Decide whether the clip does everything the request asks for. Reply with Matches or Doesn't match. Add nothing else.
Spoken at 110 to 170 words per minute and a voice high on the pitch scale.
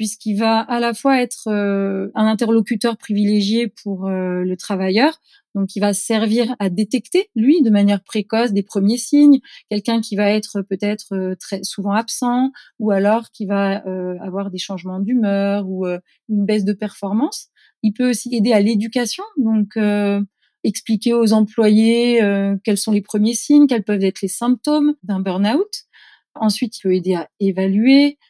Matches